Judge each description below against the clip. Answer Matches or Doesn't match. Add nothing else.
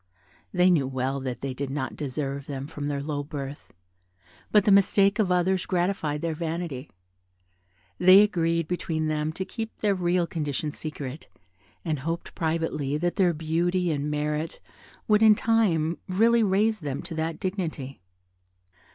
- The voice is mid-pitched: Matches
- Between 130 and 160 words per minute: Matches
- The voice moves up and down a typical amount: Matches